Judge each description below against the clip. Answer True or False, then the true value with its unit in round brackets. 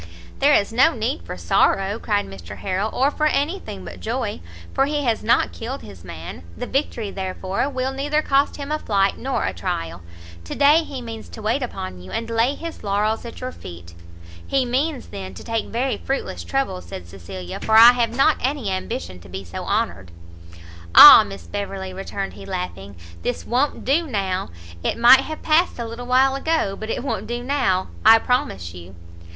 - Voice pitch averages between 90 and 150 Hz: False (225 Hz)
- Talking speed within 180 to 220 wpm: True (195 wpm)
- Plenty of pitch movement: True (6.6 semitones)